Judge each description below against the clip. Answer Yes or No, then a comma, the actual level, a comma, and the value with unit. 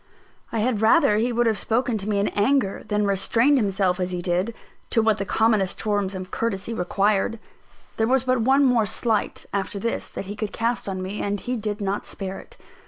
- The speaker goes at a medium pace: No, fast, 210 wpm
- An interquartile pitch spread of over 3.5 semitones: No, average, 2.9 semitones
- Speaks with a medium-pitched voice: No, high, 210 Hz